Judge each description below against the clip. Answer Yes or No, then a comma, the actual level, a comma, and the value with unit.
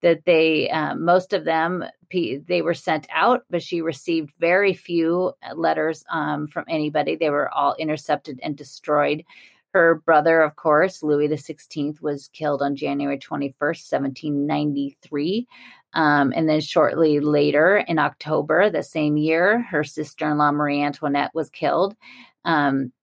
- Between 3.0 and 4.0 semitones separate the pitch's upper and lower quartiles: No, narrow, 2.4 semitones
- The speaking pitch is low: No, medium, 155 Hz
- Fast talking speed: No, average, 145 wpm